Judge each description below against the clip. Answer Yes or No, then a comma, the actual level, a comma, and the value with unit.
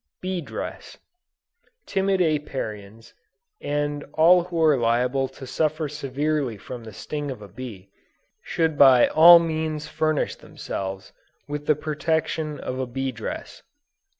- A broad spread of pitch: No, average, 4.1 semitones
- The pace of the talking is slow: Yes, slow, 130 wpm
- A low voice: No, medium, 145 Hz